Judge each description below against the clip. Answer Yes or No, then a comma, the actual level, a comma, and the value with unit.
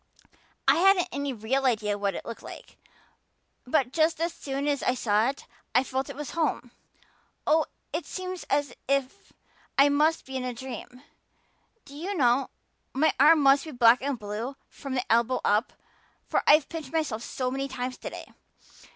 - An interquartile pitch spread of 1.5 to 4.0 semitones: Yes, average, 3.2 semitones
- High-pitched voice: Yes, very high, 270 Hz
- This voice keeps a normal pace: Yes, average, 175 wpm